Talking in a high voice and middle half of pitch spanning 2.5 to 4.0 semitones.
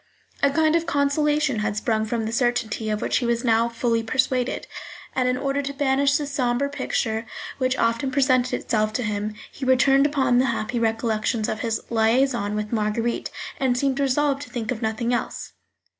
Yes: high, 245 Hz; average, 3.6 semitones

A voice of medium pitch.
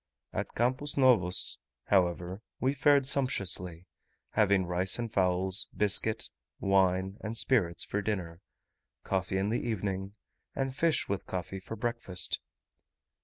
No: low, 100 Hz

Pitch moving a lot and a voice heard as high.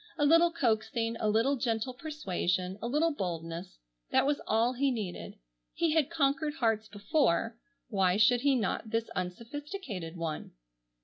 Yes: wide, 7.0 semitones; high, 230 Hz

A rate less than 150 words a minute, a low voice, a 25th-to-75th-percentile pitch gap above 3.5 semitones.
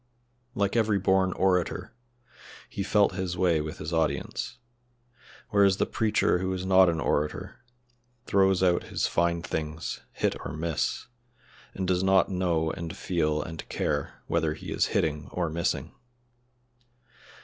No: average, 140 wpm; very low, 90 Hz; average, 3.0 semitones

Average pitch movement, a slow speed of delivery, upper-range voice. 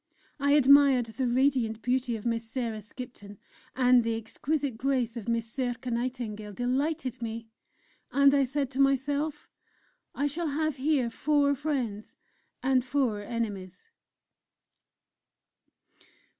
Yes: average, 3.4 semitones; slow, 120 wpm; very high, 255 Hz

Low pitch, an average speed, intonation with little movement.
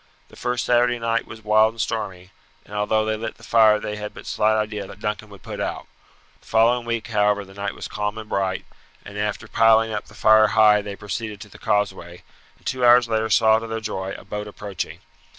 No: low, 110 Hz; fast, 220 wpm; narrow, 1.5 semitones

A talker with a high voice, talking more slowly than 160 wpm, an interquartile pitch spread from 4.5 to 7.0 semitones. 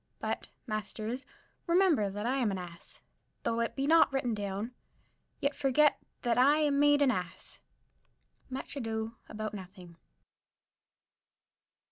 Yes: high, 235 Hz; slow, 135 wpm; average, 5.3 semitones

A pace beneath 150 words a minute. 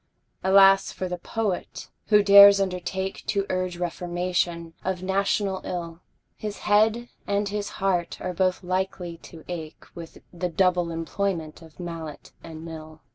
Yes: average, 140 wpm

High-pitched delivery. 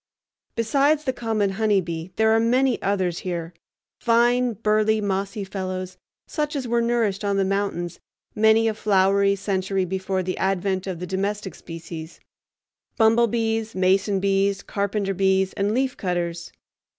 Yes: high, 200 Hz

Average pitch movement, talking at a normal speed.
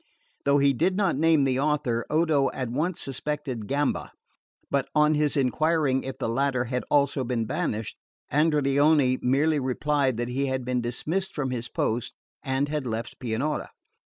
Yes: average, 3.0 semitones; average, 160 wpm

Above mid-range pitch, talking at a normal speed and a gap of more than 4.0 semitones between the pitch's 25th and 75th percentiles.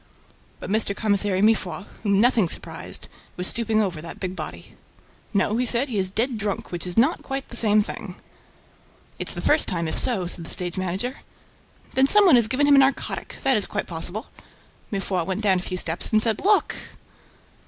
Yes: high, 210 Hz; average, 195 wpm; average, 4.5 semitones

